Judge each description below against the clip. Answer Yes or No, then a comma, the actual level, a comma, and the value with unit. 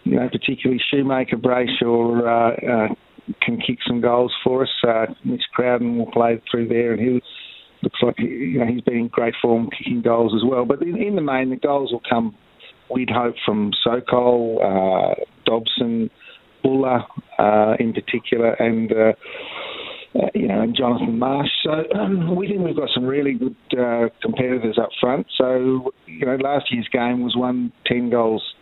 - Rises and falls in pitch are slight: Yes, narrow, 1.9 semitones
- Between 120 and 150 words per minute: No, average, 180 wpm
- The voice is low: Yes, low, 120 Hz